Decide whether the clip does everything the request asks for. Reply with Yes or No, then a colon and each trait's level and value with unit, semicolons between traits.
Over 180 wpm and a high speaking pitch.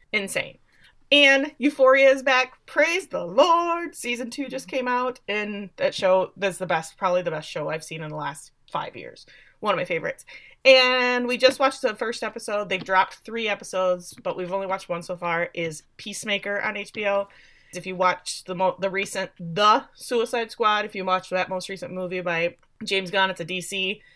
Yes: average, 195 wpm; high, 200 Hz